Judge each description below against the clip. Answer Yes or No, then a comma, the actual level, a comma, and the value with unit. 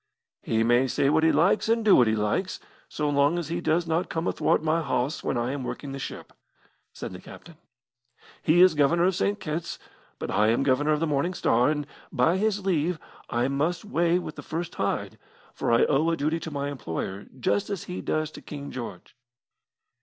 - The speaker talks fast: Yes, fast, 210 wpm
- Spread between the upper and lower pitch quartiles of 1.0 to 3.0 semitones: No, average, 4.1 semitones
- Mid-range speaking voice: Yes, medium, 155 Hz